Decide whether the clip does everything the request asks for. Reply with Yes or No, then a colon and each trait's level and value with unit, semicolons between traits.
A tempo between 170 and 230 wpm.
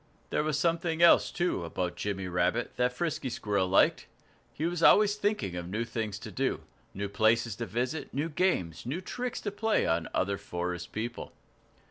Yes: average, 175 wpm